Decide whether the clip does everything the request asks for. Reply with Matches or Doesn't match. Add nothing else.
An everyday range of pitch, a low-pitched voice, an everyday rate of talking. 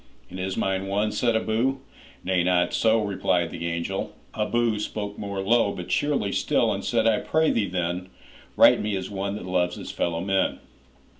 Matches